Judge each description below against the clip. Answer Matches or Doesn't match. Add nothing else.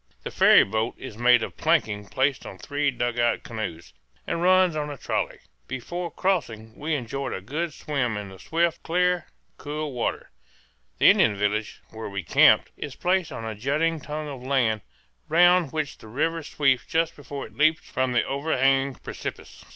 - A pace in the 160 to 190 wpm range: Matches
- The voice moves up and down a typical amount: Doesn't match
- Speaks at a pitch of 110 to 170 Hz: Matches